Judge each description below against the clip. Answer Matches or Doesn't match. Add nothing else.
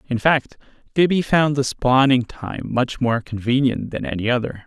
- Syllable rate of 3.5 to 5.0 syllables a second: Matches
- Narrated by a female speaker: Doesn't match